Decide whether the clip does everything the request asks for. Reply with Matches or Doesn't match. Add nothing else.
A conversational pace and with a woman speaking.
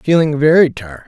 Doesn't match